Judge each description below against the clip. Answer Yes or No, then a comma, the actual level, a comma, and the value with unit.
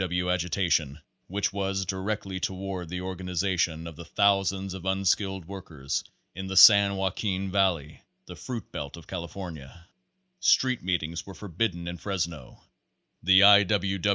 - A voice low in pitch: Yes, very low, 95 Hz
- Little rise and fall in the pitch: Yes, narrow, 2.3 semitones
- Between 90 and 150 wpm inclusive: Yes, average, 140 wpm